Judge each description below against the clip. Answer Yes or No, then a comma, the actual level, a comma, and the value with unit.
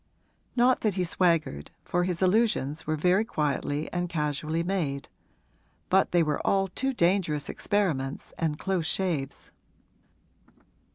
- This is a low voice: No, medium, 175 Hz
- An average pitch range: Yes, average, 4.2 semitones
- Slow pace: Yes, slow, 125 wpm